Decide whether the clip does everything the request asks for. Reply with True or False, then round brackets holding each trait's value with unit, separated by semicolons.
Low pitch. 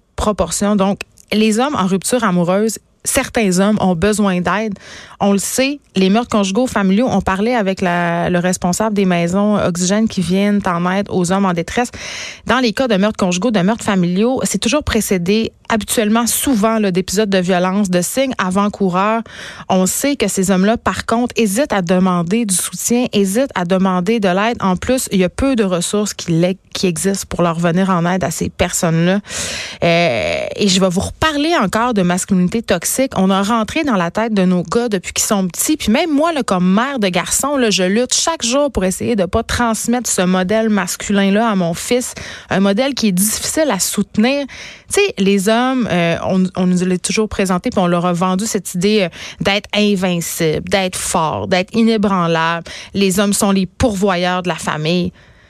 False (200 Hz)